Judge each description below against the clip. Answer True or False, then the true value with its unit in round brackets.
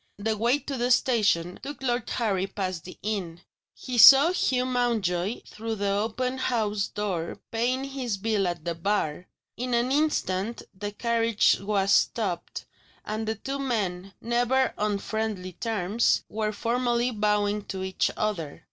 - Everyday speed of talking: True (150 wpm)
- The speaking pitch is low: False (215 Hz)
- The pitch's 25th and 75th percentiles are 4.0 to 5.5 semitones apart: False (3.6 semitones)